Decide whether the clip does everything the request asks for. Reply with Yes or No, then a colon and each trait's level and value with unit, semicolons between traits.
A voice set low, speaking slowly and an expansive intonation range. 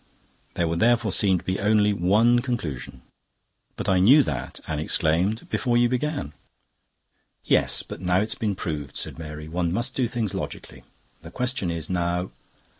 No: very low, 95 Hz; average, 165 wpm; wide, 5.9 semitones